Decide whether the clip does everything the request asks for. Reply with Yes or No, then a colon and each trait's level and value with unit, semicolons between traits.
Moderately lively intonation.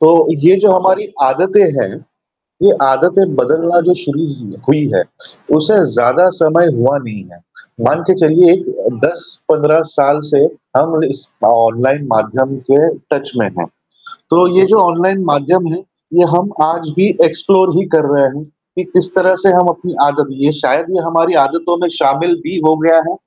Yes: average, 4.0 semitones